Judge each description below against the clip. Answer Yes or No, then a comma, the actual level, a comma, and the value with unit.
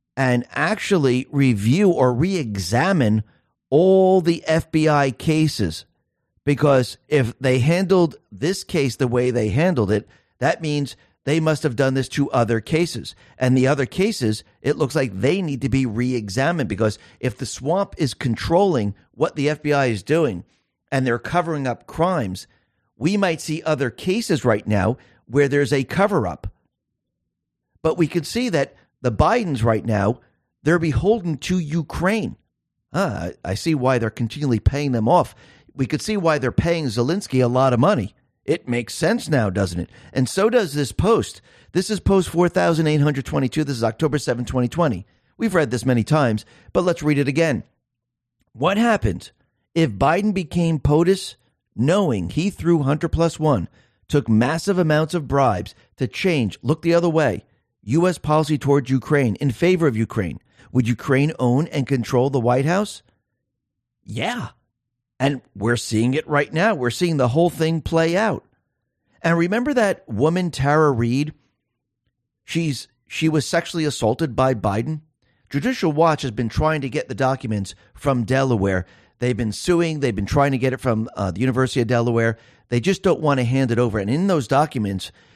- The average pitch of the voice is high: No, low, 135 Hz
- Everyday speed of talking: Yes, average, 170 wpm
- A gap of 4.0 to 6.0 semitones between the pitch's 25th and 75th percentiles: Yes, average, 5.0 semitones